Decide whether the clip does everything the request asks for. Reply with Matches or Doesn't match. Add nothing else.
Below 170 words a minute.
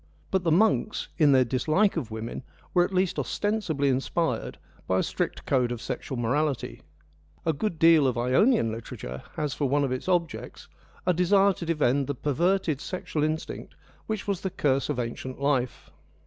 Doesn't match